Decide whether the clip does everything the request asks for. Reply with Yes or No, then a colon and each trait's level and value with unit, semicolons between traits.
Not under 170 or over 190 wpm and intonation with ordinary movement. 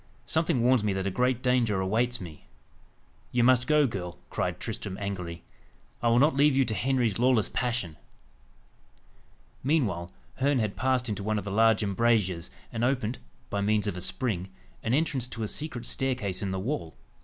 Yes: average, 180 wpm; average, 4.5 semitones